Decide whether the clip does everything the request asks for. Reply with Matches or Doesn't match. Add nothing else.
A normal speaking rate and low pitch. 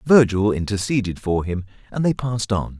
Matches